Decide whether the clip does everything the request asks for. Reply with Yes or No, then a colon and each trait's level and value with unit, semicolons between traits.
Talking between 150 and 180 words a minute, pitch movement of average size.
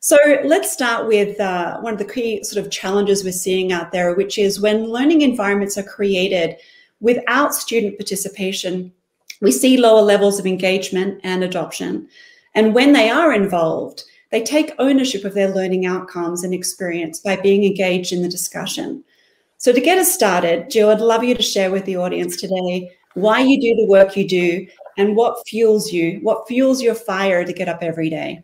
No: average, 190 wpm; average, 4.2 semitones